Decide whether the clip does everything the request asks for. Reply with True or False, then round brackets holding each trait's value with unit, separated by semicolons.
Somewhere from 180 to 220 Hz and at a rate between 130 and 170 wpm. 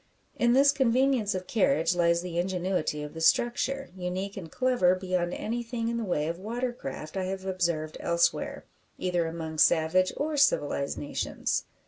True (185 Hz; 160 wpm)